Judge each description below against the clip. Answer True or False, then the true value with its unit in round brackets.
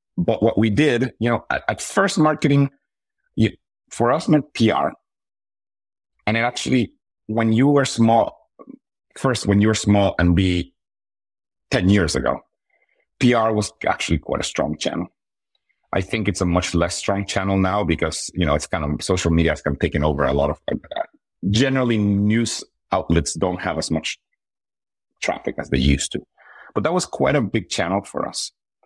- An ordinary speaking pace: True (180 wpm)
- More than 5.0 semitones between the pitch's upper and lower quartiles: True (5.4 semitones)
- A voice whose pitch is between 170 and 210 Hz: False (100 Hz)